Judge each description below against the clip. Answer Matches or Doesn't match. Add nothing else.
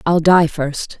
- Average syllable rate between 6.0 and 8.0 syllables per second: Doesn't match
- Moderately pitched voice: Matches